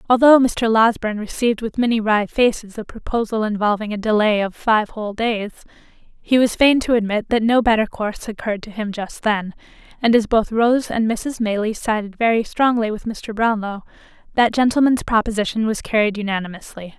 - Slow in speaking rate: No, average, 175 wpm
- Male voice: No, female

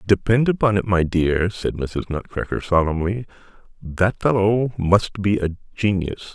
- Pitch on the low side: Yes, very low, 95 Hz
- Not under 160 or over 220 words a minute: No, average, 140 wpm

